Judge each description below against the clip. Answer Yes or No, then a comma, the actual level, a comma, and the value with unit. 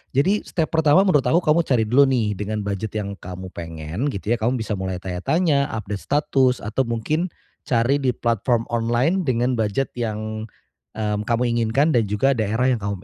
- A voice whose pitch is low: Yes, low, 115 Hz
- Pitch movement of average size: Yes, average, 4.5 semitones